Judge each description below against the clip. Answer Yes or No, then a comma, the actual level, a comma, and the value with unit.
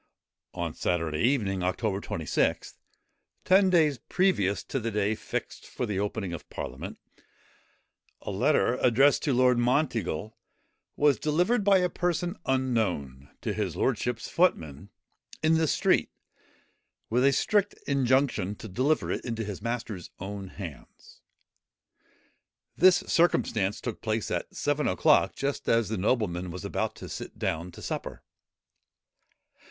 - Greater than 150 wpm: No, slow, 135 wpm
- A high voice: No, low, 115 Hz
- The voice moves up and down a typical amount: No, wide, 6.9 semitones